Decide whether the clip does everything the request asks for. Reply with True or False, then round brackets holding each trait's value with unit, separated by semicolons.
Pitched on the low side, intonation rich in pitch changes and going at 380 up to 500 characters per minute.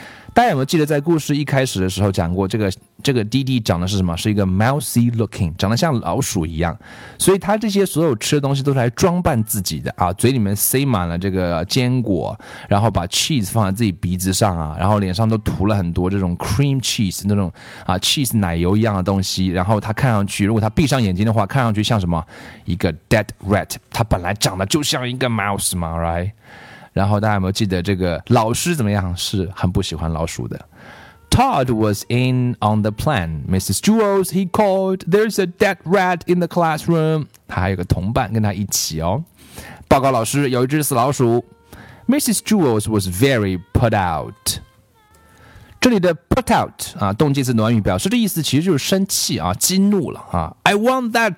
True (110 Hz; 6.8 semitones; 415 characters per minute)